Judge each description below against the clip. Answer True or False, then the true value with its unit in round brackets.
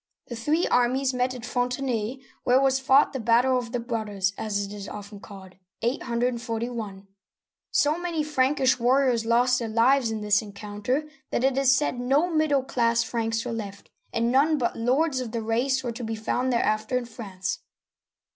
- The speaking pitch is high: True (245 Hz)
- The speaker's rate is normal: True (185 wpm)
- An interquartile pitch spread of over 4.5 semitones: False (2.8 semitones)